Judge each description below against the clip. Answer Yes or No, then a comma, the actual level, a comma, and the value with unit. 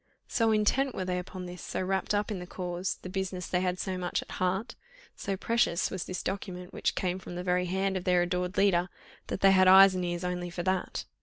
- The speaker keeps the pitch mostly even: Yes, narrow, 1.3 semitones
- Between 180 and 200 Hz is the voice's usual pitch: Yes, medium, 185 Hz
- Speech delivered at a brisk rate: Yes, fast, 235 wpm